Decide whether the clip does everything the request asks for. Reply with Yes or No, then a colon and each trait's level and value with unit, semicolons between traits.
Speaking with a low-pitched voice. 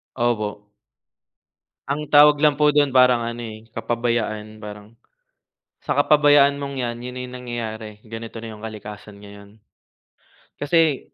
Yes: low, 120 Hz